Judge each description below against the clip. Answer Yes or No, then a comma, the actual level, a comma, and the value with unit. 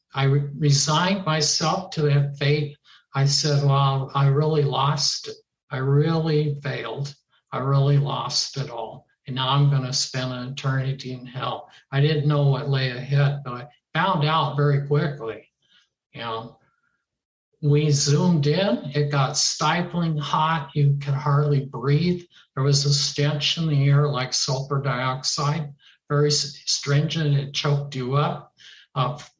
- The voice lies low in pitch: No, medium, 145 Hz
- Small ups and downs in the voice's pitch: Yes, narrow, 1.6 semitones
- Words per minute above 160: No, average, 150 wpm